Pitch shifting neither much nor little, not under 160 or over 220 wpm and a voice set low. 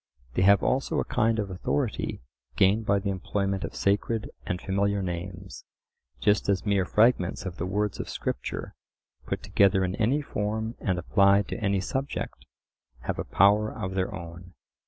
No: narrow, 2.2 semitones; average, 165 wpm; low, 100 Hz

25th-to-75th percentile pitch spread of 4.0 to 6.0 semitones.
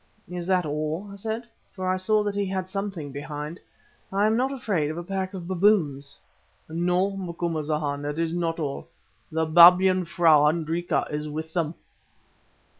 No: average, 3.6 semitones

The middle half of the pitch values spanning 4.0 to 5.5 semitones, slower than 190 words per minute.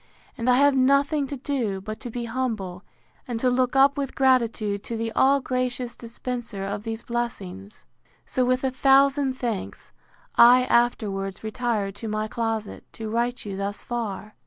No: average, 3.2 semitones; average, 165 wpm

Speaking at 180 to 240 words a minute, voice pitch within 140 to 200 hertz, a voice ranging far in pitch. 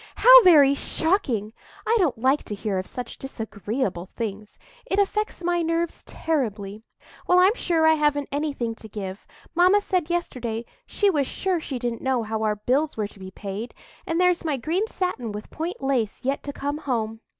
No: average, 185 wpm; very high, 275 Hz; wide, 7.4 semitones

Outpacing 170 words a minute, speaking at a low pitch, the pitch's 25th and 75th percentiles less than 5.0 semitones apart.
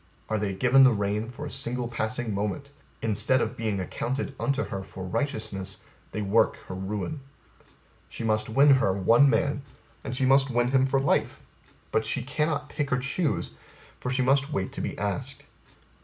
Yes: average, 180 wpm; low, 120 Hz; average, 4.4 semitones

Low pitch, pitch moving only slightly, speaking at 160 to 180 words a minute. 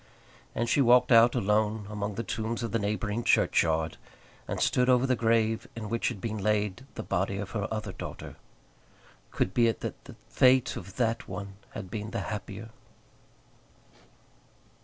Yes: low, 110 Hz; narrow, 2.3 semitones; average, 165 wpm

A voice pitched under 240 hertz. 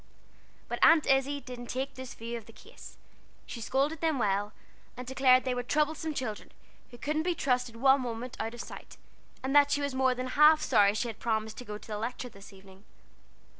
No: very high, 255 Hz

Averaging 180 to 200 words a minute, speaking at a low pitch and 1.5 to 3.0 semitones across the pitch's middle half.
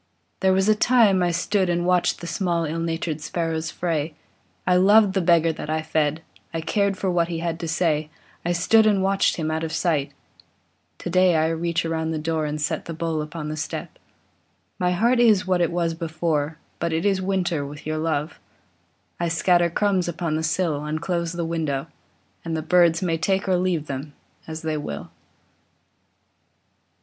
No: average, 190 wpm; medium, 165 Hz; narrow, 2.4 semitones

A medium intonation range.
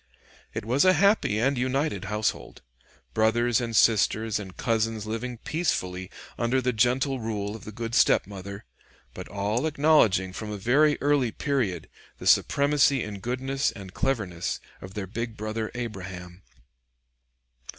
Yes: average, 4.4 semitones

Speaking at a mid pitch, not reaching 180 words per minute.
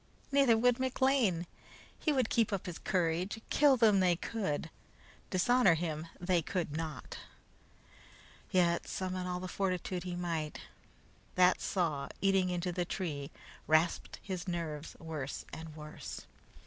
Yes: medium, 180 Hz; slow, 135 wpm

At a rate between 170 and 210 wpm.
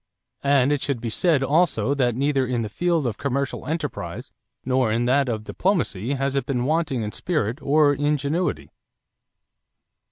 No: average, 160 wpm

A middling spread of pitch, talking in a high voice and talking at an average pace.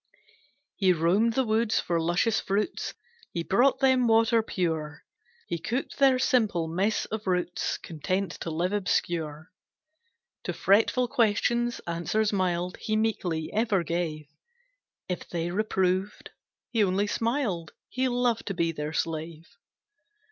No: average, 4.9 semitones; high, 195 Hz; slow, 130 wpm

